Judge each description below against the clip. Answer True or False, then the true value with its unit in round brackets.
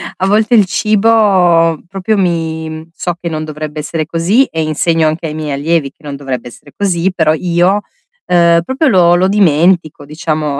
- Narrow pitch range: False (3.5 semitones)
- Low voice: False (170 Hz)